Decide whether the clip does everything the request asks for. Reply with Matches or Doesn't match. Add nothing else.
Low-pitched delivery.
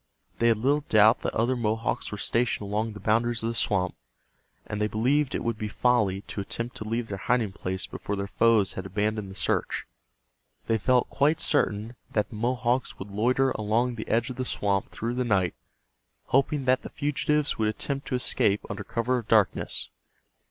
Matches